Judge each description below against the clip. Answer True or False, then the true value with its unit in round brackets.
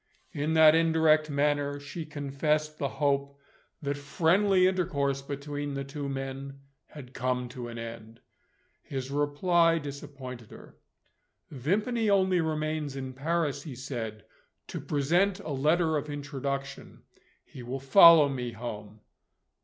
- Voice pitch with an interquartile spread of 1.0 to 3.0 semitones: True (2.7 semitones)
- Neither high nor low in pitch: True (145 Hz)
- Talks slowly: True (130 wpm)